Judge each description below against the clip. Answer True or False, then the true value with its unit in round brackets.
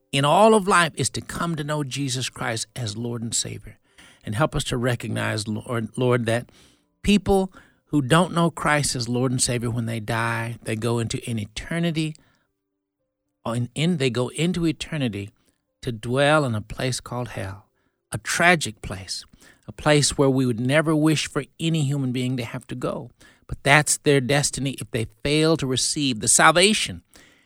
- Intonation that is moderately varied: True (4.5 semitones)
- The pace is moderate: True (180 wpm)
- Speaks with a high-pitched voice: False (130 Hz)